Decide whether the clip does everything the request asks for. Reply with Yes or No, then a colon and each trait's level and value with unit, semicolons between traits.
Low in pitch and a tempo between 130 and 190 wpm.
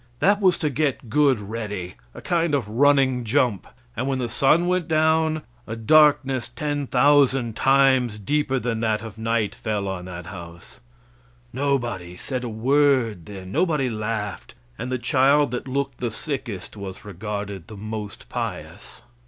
Yes: low, 120 Hz; average, 155 wpm